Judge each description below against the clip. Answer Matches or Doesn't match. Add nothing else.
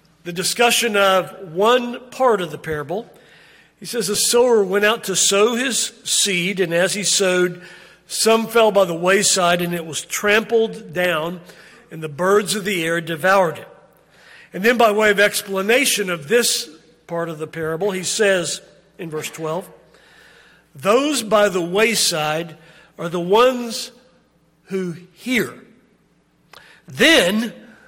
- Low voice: Doesn't match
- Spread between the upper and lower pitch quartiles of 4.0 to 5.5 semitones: Matches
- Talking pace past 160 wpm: Doesn't match